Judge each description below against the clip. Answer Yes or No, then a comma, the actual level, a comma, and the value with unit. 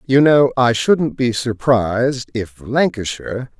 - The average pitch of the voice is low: Yes, low, 125 Hz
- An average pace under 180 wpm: Yes, slow, 135 wpm